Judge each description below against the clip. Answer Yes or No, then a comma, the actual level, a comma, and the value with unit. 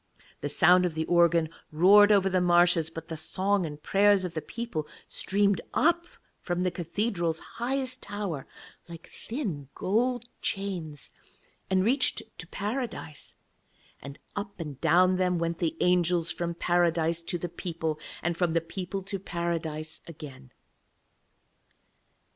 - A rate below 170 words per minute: Yes, average, 140 wpm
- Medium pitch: Yes, medium, 175 Hz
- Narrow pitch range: No, average, 3.3 semitones